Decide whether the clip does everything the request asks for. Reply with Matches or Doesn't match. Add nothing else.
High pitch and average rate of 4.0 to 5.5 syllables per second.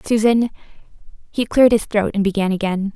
Doesn't match